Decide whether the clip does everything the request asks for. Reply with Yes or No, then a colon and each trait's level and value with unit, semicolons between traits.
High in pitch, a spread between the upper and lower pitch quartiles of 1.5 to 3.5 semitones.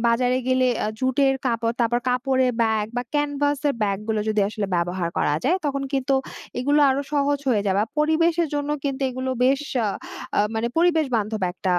No: very high, 255 Hz; average, 4.5 semitones